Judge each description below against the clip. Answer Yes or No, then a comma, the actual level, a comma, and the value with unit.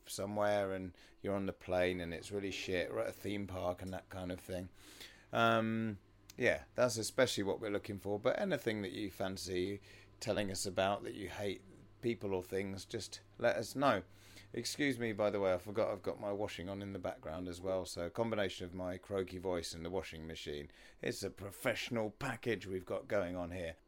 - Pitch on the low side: Yes, very low, 95 Hz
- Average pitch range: No, narrow, 2.2 semitones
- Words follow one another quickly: Yes, fast, 210 wpm